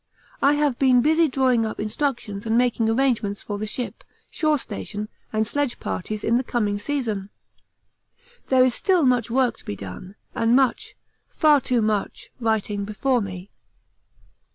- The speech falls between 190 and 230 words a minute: No, average, 155 wpm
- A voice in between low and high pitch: No, high, 235 Hz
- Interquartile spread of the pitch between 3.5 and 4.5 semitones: Yes, average, 3.9 semitones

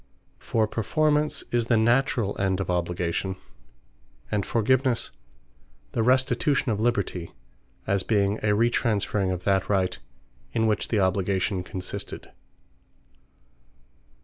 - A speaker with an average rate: No, slow, 110 wpm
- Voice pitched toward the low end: Yes, low, 105 Hz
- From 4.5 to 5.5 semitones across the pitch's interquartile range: No, average, 3.8 semitones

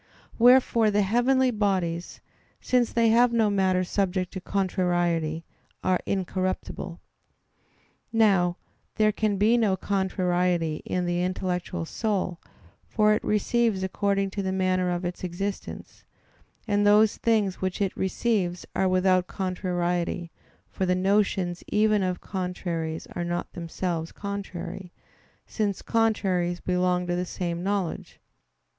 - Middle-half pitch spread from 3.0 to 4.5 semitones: No, narrow, 2.5 semitones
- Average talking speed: No, slow, 125 wpm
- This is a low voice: No, medium, 185 Hz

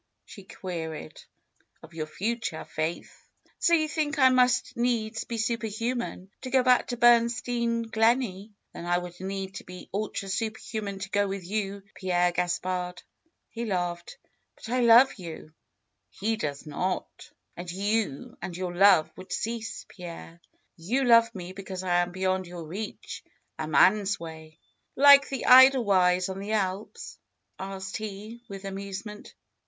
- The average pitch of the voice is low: No, high, 195 Hz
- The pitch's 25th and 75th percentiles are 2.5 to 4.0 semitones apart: No, average, 4.4 semitones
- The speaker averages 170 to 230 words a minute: No, average, 150 wpm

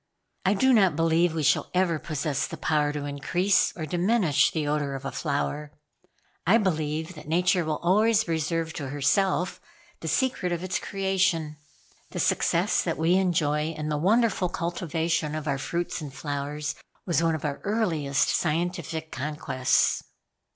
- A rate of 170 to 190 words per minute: No, average, 160 wpm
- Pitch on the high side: No, medium, 160 Hz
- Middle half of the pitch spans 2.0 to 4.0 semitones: Yes, average, 3.3 semitones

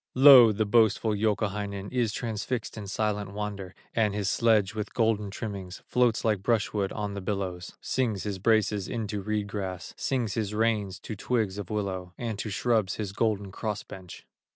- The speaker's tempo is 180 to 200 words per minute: No, average, 170 wpm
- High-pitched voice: No, low, 105 Hz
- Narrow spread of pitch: Yes, narrow, 2.1 semitones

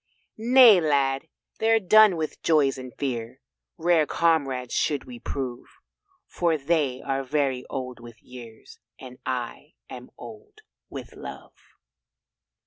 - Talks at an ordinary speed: No, slow, 125 wpm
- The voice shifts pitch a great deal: No, average, 4.8 semitones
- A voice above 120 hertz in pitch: Yes, medium, 140 Hz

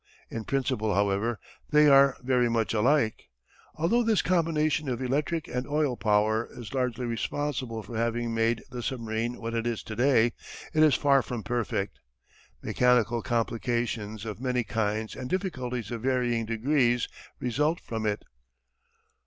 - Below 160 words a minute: Yes, average, 145 wpm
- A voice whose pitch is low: Yes, low, 120 Hz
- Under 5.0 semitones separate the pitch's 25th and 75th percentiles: Yes, average, 3.2 semitones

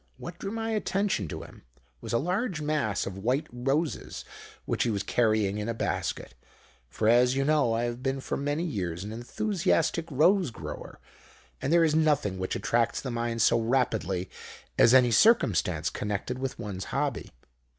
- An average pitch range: No, wide, 5.9 semitones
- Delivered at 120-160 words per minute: No, average, 170 wpm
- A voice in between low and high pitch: No, low, 125 Hz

